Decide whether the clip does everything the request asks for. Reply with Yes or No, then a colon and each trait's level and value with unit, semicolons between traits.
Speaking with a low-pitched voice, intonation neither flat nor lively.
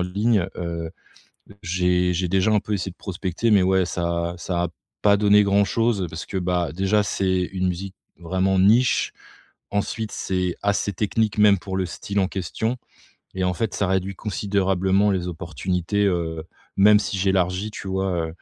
No: very low, 95 Hz; narrow, 2.3 semitones